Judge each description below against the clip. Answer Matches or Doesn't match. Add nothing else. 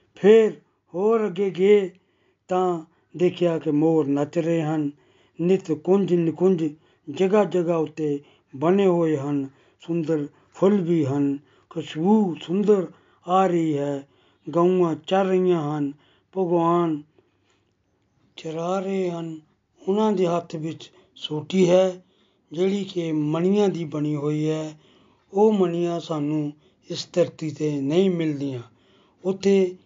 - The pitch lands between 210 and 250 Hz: Doesn't match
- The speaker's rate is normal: Matches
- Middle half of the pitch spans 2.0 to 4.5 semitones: Matches